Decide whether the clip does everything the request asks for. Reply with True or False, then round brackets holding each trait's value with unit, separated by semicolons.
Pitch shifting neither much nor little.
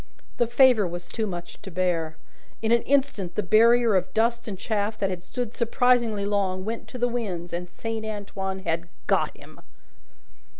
True (4.1 semitones)